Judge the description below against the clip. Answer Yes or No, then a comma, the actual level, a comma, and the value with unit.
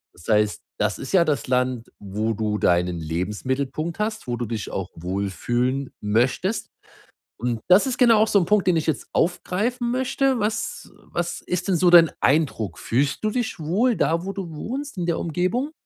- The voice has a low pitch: No, medium, 160 Hz